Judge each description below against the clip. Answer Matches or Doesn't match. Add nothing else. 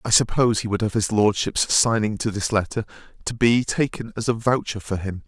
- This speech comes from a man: Matches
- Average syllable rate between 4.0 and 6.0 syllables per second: Matches